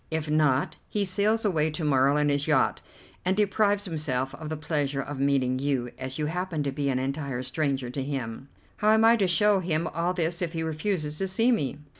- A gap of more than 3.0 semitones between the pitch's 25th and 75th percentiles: Yes, average, 4.9 semitones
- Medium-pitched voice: Yes, medium, 155 Hz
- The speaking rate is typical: No, fast, 215 wpm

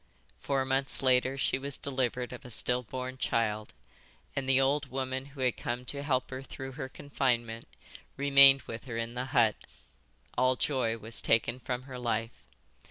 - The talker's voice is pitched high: No, low, 130 Hz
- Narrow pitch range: Yes, narrow, 2.0 semitones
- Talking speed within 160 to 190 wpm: Yes, average, 170 wpm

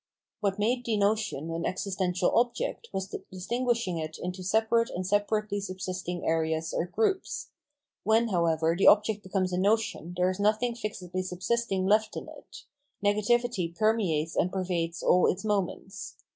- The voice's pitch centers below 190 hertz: No, high, 195 Hz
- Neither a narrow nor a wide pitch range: Yes, average, 3.5 semitones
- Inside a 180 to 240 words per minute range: No, average, 155 wpm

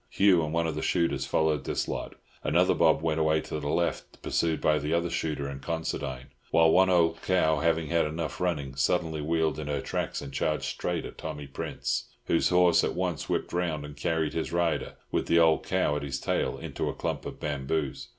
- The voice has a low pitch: Yes, very low, 80 Hz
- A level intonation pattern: Yes, narrow, 2.2 semitones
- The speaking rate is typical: No, fast, 210 wpm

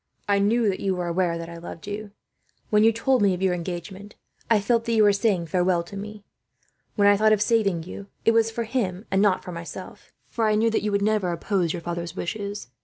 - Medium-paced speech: No, fast, 240 wpm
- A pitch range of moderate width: Yes, average, 3.3 semitones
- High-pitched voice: Yes, high, 200 Hz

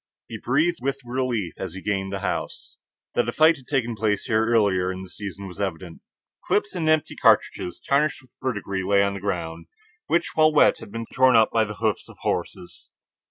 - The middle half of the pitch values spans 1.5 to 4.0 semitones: No, average, 5.3 semitones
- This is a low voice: Yes, low, 110 Hz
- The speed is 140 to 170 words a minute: No, fast, 205 wpm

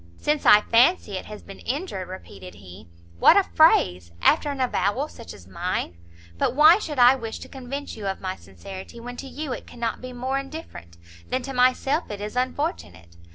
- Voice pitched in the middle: No, high, 245 Hz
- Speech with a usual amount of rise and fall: No, wide, 6.4 semitones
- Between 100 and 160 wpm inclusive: No, average, 195 wpm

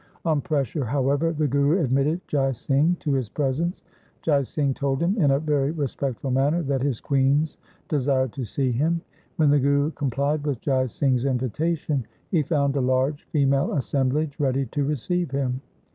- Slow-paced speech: No, average, 175 wpm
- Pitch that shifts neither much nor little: No, narrow, 2.2 semitones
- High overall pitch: No, medium, 140 Hz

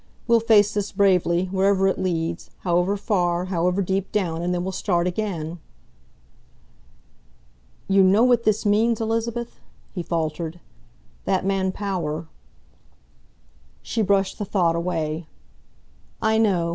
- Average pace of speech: No, slow, 130 wpm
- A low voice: No, high, 190 Hz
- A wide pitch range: No, average, 3.1 semitones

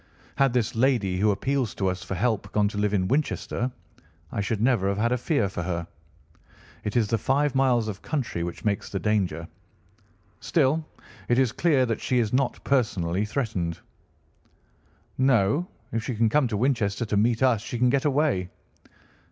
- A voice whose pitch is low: Yes, low, 115 Hz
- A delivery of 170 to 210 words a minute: Yes, average, 180 wpm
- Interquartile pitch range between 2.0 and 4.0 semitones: No, average, 4.6 semitones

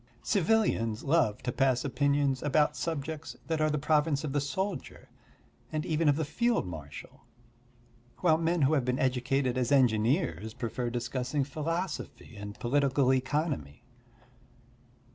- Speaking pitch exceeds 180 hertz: No, medium, 140 Hz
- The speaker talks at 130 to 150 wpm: Yes, slow, 135 wpm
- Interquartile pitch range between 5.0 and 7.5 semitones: No, average, 3.8 semitones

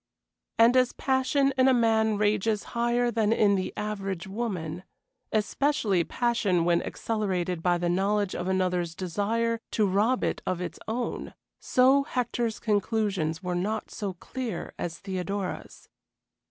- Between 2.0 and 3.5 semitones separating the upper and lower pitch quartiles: No, average, 4.0 semitones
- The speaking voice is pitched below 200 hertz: No, high, 210 Hz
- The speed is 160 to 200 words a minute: No, average, 140 wpm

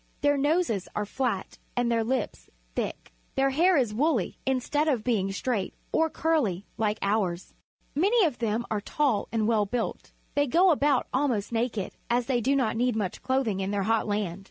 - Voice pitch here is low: No, high, 235 Hz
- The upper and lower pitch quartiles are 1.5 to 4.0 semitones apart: No, average, 5.0 semitones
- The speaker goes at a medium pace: Yes, average, 180 wpm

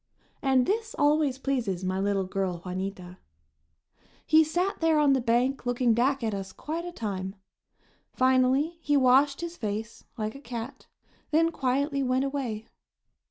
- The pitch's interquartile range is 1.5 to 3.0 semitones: No, average, 5.3 semitones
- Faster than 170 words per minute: No, average, 150 wpm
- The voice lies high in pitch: Yes, very high, 255 Hz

